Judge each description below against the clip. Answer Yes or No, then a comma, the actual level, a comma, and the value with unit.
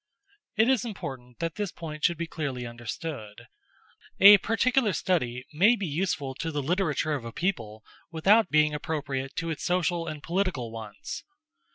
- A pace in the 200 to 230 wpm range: No, average, 160 wpm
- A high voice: No, medium, 160 Hz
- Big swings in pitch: Yes, wide, 5.8 semitones